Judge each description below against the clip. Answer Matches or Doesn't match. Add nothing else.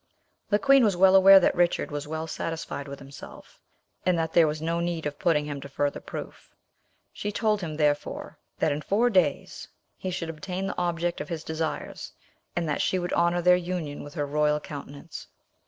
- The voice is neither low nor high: Matches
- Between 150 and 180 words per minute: Doesn't match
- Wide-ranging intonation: Doesn't match